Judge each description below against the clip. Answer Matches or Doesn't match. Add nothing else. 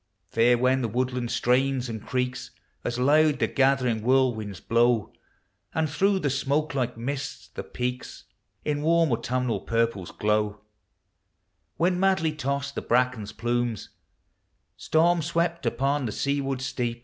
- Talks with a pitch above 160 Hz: Doesn't match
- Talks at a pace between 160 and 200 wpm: Doesn't match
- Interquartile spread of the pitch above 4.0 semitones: Doesn't match